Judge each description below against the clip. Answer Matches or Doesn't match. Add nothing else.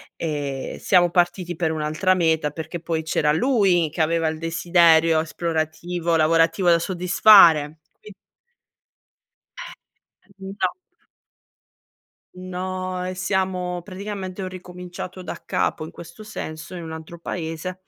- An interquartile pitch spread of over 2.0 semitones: Matches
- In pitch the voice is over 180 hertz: Doesn't match